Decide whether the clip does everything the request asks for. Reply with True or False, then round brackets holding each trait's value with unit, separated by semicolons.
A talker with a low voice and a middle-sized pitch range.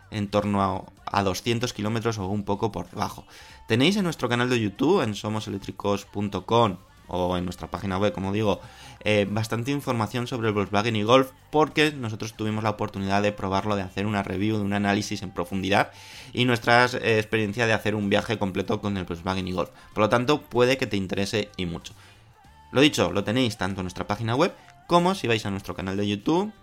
True (105 Hz; 3.1 semitones)